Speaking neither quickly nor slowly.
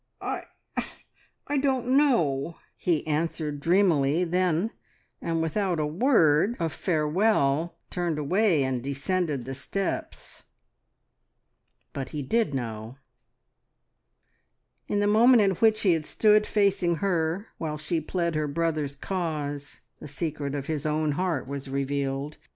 No: slow, 125 wpm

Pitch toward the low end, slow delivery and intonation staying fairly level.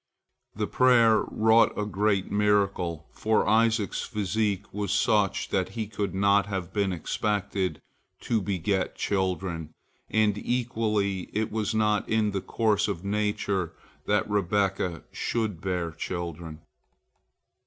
Yes: low, 100 Hz; slow, 120 wpm; narrow, 2.3 semitones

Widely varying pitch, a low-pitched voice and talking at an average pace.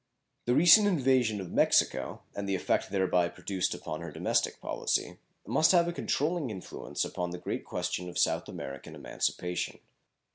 Yes: wide, 8.7 semitones; low, 100 Hz; average, 155 wpm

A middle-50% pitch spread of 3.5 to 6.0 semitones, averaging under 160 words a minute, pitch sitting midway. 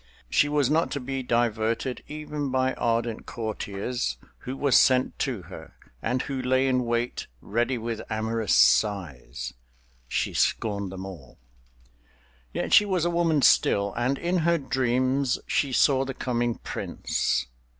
No: average, 4.7 semitones; average, 140 wpm; low, 120 Hz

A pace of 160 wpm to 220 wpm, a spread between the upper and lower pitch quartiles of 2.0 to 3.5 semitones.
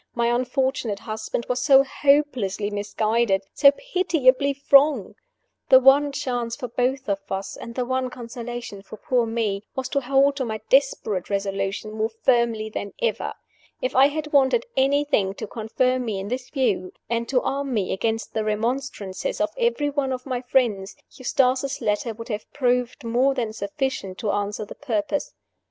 No: average, 165 wpm; average, 3.9 semitones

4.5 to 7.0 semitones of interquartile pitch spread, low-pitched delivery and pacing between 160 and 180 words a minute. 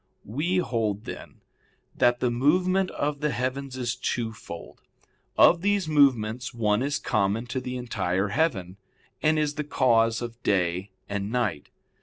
No: average, 5.2 semitones; low, 125 Hz; average, 145 wpm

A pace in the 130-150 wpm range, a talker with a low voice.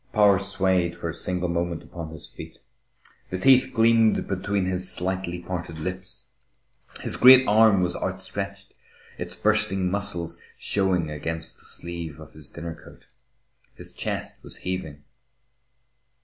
Yes: slow, 135 wpm; very low, 90 Hz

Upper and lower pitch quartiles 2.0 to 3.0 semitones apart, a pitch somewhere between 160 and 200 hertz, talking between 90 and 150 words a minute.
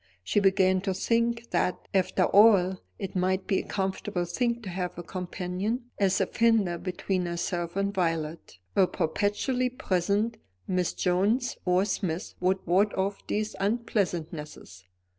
Yes: narrow, 2.6 semitones; high, 190 Hz; average, 140 wpm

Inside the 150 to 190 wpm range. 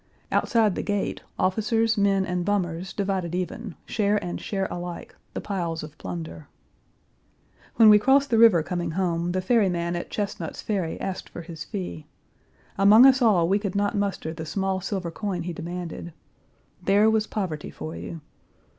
Yes: average, 165 wpm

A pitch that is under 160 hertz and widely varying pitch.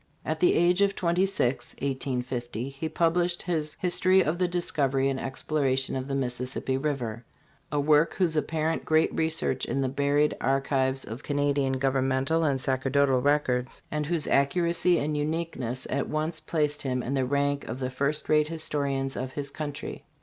No: medium, 140 Hz; average, 3.0 semitones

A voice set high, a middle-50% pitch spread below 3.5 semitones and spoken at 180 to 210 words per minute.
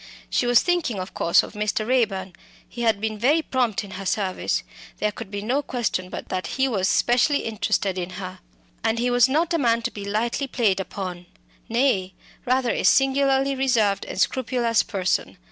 No: high, 225 Hz; average, 4.9 semitones; average, 185 wpm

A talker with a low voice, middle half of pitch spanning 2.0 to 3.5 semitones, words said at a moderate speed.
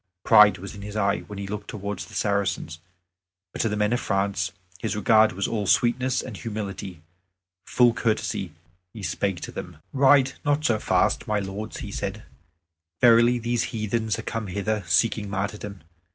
Yes: low, 105 Hz; narrow, 2.4 semitones; average, 170 wpm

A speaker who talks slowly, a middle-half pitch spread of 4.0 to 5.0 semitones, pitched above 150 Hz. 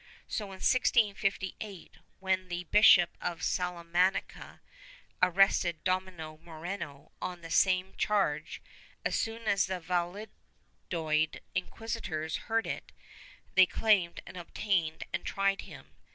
No: slow, 115 wpm; narrow, 2.5 semitones; medium, 185 Hz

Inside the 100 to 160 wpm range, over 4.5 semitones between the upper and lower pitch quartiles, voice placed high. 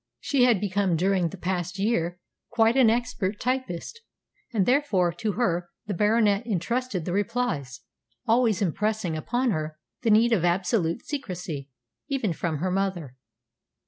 Yes: average, 145 wpm; average, 5.0 semitones; high, 200 Hz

